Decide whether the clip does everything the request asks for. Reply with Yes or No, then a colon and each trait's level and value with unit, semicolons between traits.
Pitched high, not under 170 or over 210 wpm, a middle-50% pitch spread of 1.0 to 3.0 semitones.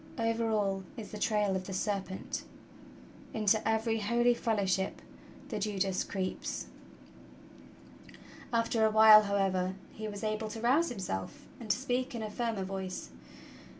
No: high, 215 Hz; average, 140 wpm; average, 2.7 semitones